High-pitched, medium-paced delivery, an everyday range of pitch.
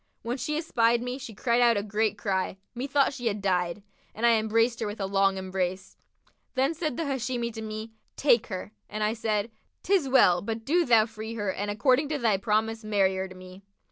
No: high, 220 Hz; fast, 210 wpm; average, 3.5 semitones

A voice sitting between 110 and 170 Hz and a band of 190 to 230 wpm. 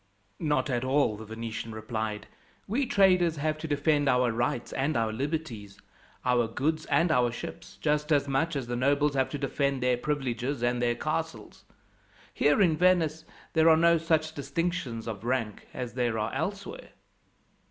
No: medium, 140 Hz; average, 165 wpm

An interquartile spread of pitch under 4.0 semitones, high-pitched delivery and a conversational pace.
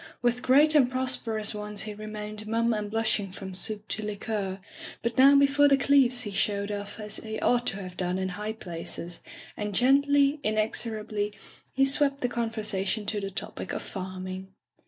Yes: average, 3.5 semitones; high, 215 Hz; average, 180 wpm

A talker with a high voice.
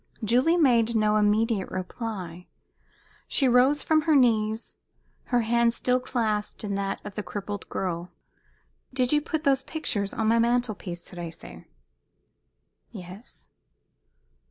Yes: high, 225 Hz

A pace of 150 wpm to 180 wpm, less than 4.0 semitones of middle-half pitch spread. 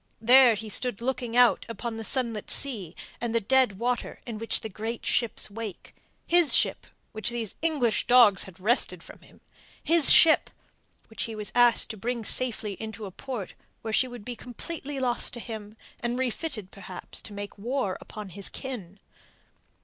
Yes: average, 170 wpm; average, 2.9 semitones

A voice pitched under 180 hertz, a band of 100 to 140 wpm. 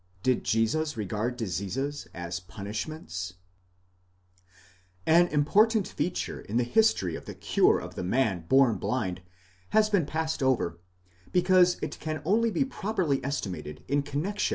Yes: low, 135 Hz; slow, 135 wpm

